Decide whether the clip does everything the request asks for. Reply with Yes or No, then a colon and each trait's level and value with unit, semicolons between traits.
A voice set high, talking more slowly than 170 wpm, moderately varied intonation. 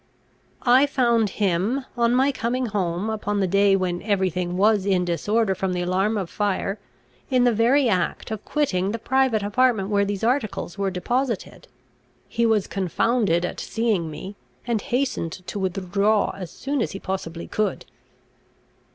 Yes: high, 205 Hz; average, 160 wpm; average, 3.9 semitones